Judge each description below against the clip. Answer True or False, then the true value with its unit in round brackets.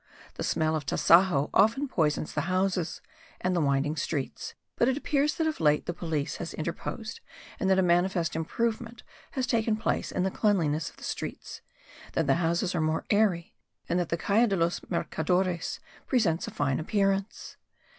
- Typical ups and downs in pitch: True (4.8 semitones)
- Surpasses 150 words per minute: True (175 wpm)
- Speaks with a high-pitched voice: False (180 Hz)